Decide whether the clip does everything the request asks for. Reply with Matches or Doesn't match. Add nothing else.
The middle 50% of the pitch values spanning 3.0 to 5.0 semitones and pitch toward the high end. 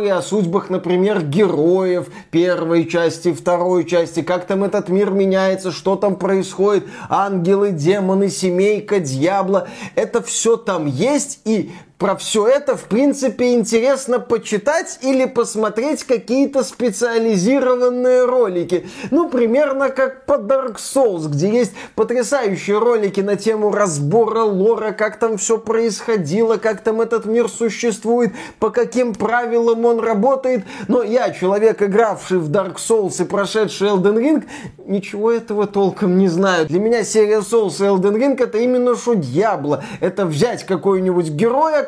Matches